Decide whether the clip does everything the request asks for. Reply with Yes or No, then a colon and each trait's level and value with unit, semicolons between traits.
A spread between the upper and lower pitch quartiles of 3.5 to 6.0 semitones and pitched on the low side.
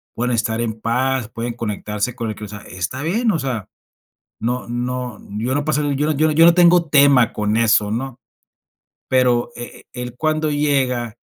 Yes: average, 3.8 semitones; low, 125 Hz